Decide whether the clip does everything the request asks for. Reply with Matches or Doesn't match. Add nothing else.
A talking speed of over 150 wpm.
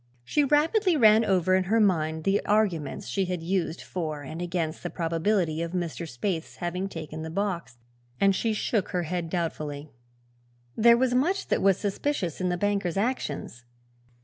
Matches